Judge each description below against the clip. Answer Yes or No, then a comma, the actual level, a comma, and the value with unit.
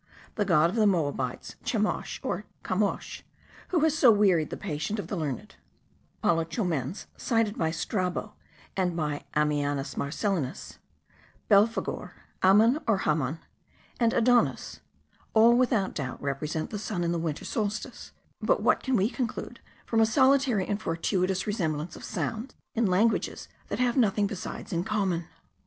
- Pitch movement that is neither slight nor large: No, wide, 5.7 semitones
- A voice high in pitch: Yes, high, 195 Hz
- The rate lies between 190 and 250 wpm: No, average, 145 wpm